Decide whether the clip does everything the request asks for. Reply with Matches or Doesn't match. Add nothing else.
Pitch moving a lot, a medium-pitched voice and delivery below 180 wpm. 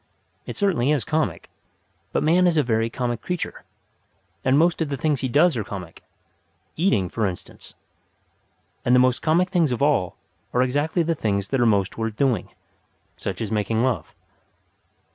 Doesn't match